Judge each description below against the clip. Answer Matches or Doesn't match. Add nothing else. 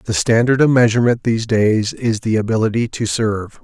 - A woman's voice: Doesn't match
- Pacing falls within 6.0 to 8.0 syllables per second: Doesn't match